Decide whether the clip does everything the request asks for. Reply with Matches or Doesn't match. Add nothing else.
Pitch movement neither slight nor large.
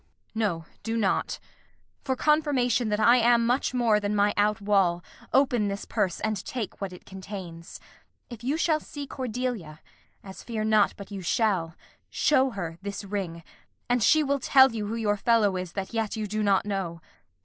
Matches